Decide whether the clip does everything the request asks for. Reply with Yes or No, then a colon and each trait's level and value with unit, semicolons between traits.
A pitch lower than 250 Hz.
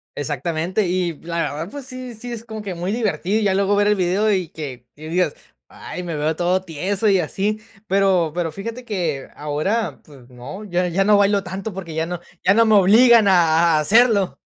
Yes: medium, 185 Hz